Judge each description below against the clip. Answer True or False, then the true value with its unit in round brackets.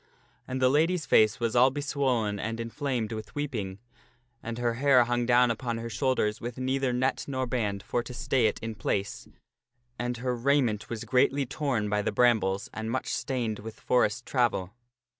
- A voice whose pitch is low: True (120 Hz)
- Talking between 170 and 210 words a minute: True (180 wpm)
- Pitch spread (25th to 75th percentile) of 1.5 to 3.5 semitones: True (2.8 semitones)